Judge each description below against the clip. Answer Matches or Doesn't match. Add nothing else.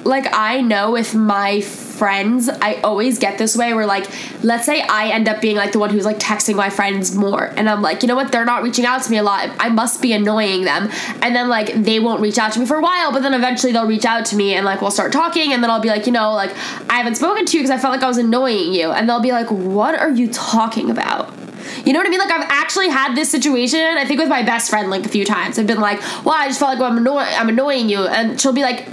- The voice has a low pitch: Doesn't match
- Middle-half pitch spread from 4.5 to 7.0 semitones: Doesn't match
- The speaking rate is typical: Doesn't match